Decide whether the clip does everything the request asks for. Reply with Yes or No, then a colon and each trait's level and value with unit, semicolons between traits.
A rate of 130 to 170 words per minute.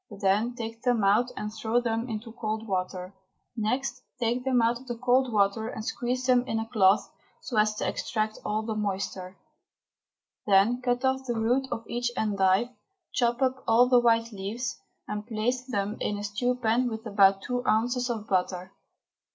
No: average, 180 wpm